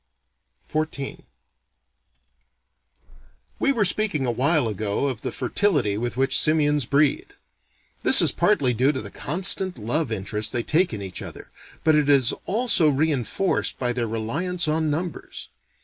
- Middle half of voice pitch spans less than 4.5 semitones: No, average, 5.2 semitones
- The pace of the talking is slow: No, average, 145 wpm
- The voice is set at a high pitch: No, medium, 140 Hz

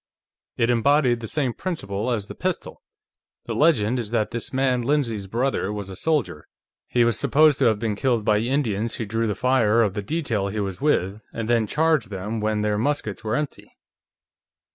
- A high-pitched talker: No, low, 115 Hz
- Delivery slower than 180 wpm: No, average, 190 wpm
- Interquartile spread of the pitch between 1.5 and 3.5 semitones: No, average, 4.0 semitones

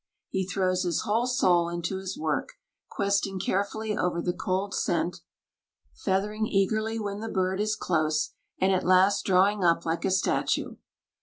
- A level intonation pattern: Yes, narrow, 2.3 semitones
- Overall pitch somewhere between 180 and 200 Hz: Yes, high, 190 Hz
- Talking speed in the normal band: Yes, average, 155 wpm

